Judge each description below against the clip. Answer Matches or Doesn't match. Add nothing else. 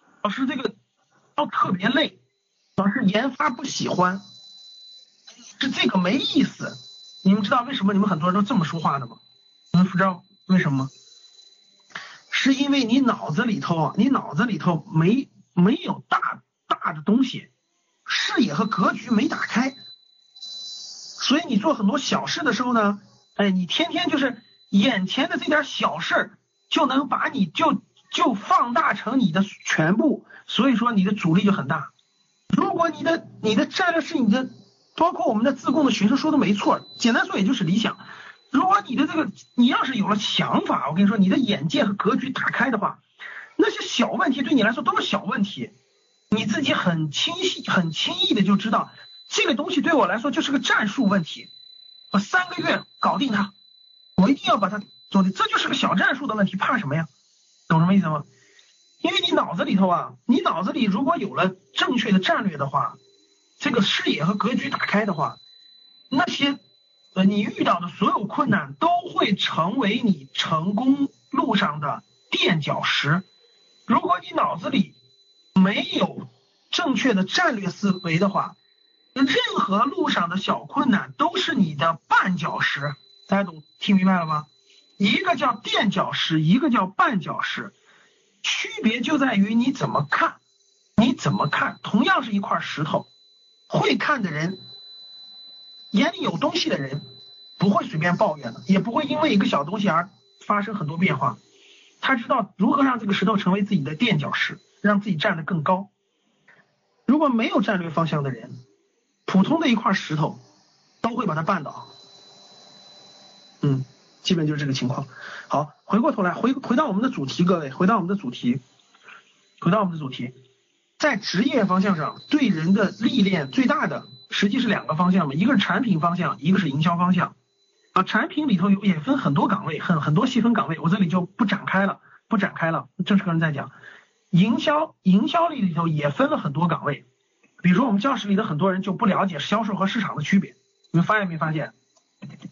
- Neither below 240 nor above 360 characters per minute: Matches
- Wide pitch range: Matches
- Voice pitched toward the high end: Matches